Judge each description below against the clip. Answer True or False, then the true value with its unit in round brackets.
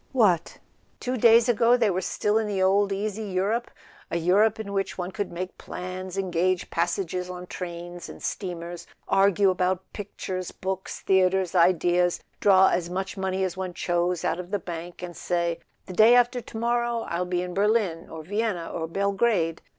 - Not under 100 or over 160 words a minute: False (180 wpm)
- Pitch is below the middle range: False (185 Hz)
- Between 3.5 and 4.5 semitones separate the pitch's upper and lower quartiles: False (2.7 semitones)